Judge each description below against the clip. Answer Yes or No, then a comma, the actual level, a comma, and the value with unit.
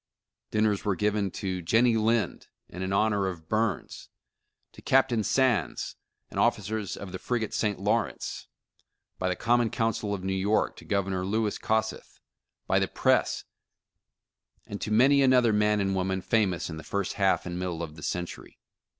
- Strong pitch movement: No, average, 2.9 semitones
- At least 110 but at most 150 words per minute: No, average, 165 wpm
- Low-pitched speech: Yes, low, 105 Hz